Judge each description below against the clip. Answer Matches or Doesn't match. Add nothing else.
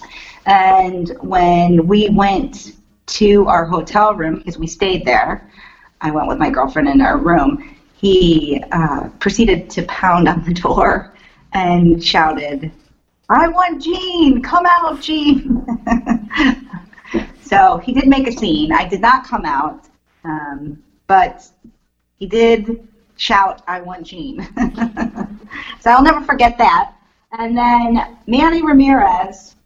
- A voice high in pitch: Matches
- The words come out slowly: Matches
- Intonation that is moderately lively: Doesn't match